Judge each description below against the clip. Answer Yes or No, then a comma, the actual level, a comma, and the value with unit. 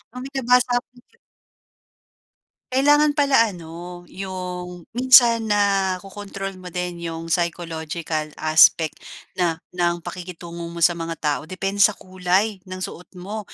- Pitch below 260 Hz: Yes, medium, 185 Hz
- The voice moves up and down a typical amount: Yes, average, 3.3 semitones